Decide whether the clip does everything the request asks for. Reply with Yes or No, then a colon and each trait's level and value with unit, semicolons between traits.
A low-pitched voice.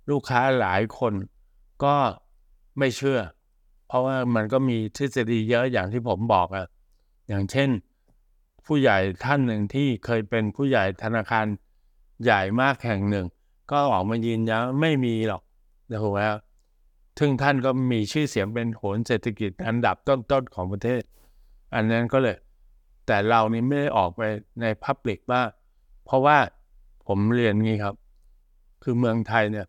Yes: low, 115 Hz